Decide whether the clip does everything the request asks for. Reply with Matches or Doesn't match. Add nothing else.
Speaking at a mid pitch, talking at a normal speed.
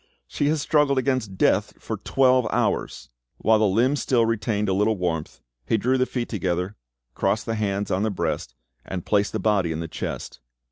Doesn't match